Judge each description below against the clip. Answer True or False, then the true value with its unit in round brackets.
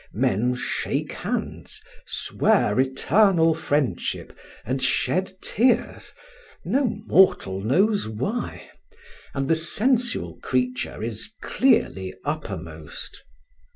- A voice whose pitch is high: False (145 Hz)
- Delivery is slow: True (85 wpm)